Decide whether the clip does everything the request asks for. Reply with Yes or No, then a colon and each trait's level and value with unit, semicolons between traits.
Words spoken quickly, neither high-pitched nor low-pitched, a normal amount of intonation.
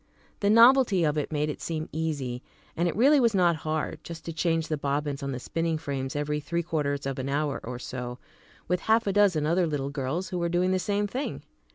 Yes: fast, 225 wpm; medium, 160 Hz; average, 4.1 semitones